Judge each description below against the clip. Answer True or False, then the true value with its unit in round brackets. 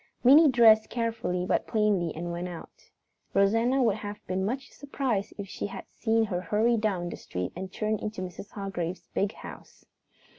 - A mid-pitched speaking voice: False (205 Hz)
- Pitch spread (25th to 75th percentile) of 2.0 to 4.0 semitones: True (3.6 semitones)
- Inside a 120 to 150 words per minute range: False (175 wpm)